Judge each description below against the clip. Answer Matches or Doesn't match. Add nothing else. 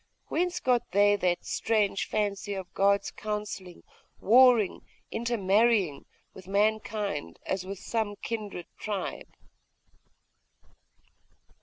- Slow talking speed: Matches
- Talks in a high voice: Matches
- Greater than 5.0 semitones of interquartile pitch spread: Doesn't match